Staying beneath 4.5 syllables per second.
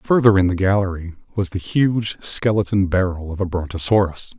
No: 5.1 syllables/s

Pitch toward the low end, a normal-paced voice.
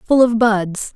No: high, 220 Hz; average, 190 wpm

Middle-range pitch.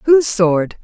No: high, 220 Hz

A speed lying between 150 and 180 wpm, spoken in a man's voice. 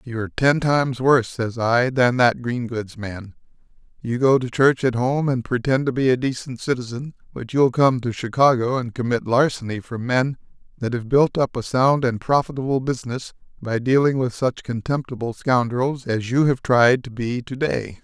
No: average, 195 wpm; male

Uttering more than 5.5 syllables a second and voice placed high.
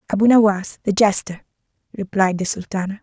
Yes: 5.8 syllables/s; high, 200 Hz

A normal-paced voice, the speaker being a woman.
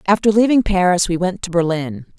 Yes: average, 190 wpm; female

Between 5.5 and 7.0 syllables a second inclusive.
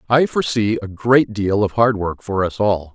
No: 4.8 syllables/s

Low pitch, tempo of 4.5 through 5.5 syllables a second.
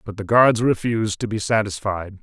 Yes: low, 105 Hz; 5.2 syllables/s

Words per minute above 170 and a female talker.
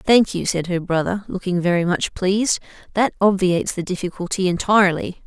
No: average, 160 wpm; female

